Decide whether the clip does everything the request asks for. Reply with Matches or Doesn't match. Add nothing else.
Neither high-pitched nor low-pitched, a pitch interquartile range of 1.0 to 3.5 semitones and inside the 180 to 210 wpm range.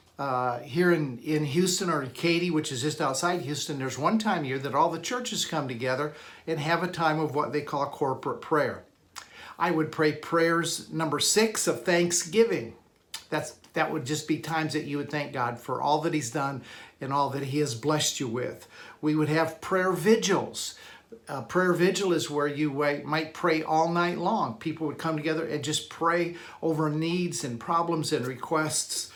Matches